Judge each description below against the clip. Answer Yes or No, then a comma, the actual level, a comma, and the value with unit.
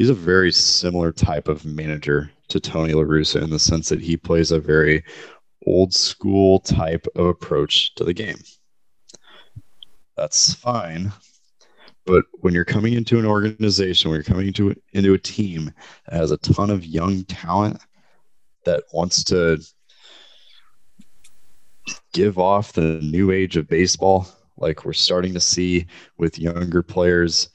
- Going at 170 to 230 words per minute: No, average, 145 wpm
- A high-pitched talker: No, very low, 90 Hz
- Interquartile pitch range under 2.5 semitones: No, average, 2.9 semitones